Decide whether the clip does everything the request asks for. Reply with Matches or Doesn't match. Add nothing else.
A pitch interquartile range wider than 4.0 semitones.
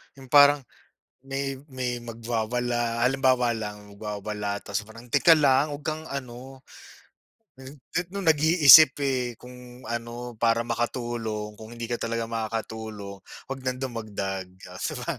Doesn't match